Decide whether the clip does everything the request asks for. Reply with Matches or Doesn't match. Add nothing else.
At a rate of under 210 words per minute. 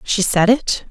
Matches